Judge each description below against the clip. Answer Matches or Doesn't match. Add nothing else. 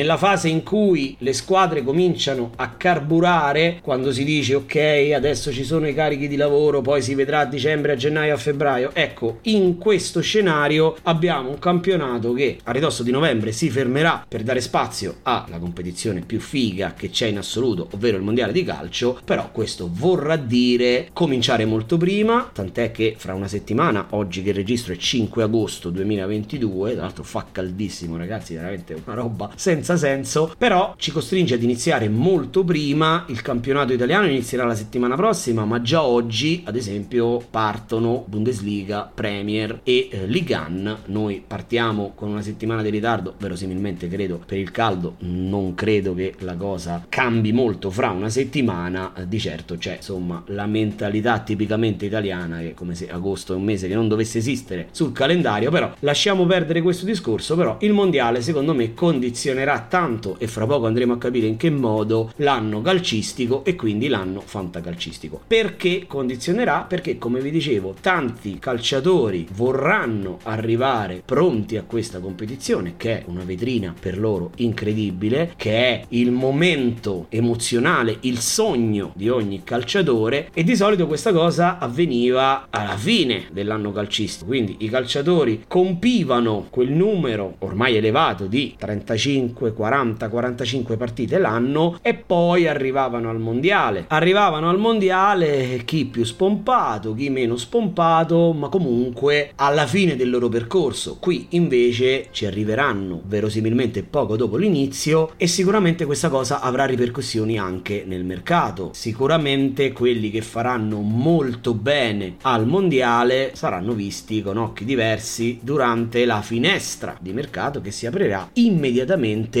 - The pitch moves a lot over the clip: Matches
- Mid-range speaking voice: Doesn't match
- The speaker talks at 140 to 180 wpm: Matches